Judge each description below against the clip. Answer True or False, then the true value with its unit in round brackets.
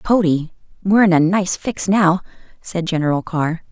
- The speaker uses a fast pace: False (160 wpm)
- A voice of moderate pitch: True (175 Hz)